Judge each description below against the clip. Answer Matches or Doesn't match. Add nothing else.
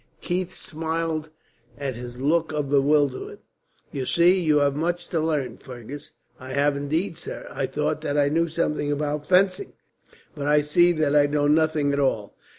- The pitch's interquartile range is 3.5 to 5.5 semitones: Doesn't match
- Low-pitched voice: Doesn't match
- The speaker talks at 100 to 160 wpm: Doesn't match